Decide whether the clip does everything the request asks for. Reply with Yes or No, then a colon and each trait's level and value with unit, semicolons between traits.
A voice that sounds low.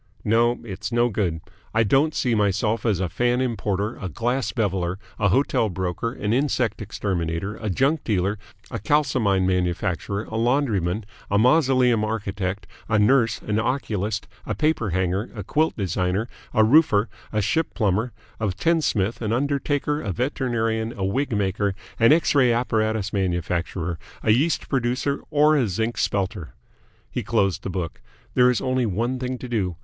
Yes: low, 110 Hz